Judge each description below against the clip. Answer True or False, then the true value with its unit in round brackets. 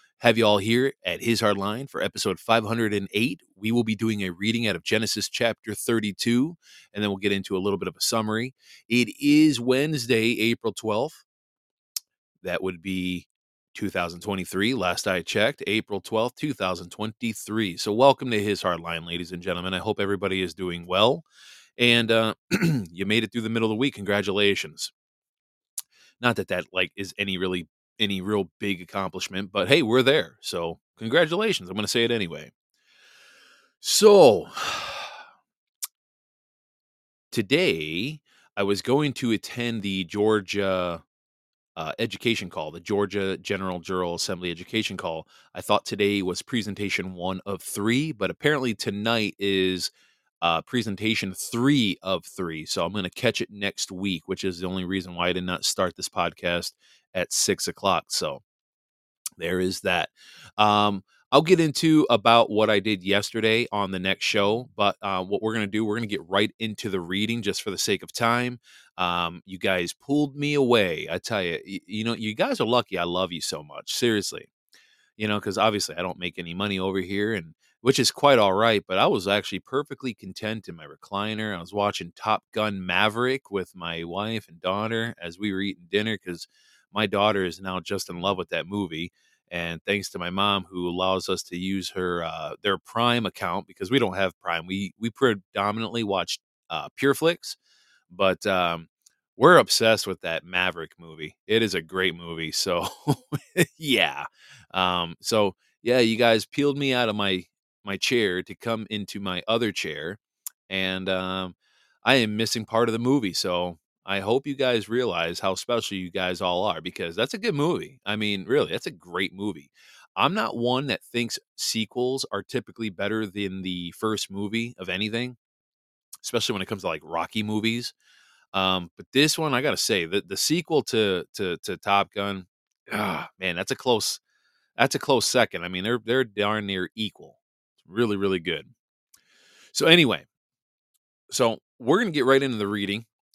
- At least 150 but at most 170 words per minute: False (180 wpm)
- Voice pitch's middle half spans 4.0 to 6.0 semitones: False (3.5 semitones)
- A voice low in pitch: True (100 Hz)